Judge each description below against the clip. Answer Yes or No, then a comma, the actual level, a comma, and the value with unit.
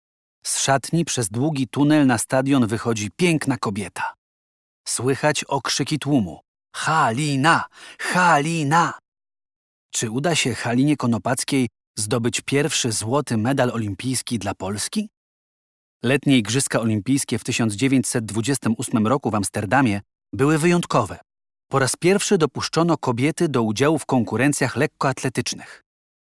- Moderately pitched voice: No, low, 130 Hz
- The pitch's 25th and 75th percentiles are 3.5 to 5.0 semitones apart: Yes, average, 4.2 semitones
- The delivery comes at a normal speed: No, slow, 105 wpm